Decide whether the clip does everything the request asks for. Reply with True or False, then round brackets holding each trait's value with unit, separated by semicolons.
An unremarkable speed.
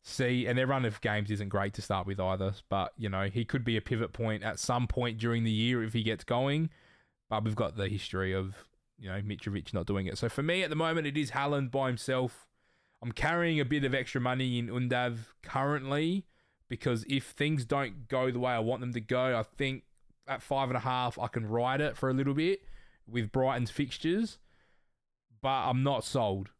False (220 wpm)